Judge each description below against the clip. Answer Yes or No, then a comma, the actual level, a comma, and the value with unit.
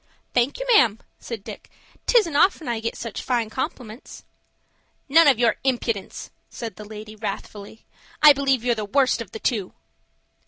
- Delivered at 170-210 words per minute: No, average, 160 wpm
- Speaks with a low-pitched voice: No, high, 235 Hz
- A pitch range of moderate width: Yes, average, 4.1 semitones